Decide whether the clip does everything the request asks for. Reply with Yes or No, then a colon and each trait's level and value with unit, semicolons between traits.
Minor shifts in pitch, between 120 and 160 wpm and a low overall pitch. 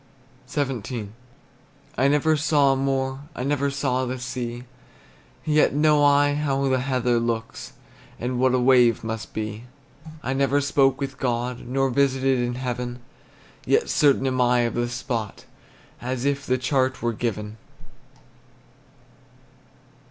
Yes: narrow, 2.3 semitones; slow, 135 wpm; low, 130 Hz